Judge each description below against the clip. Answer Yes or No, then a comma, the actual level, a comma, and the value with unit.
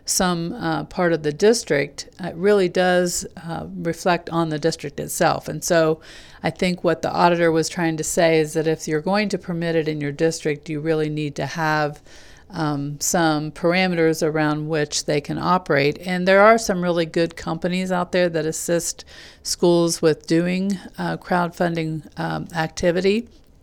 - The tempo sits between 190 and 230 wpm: No, average, 175 wpm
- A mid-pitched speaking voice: Yes, medium, 165 Hz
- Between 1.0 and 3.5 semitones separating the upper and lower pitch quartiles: Yes, narrow, 2.5 semitones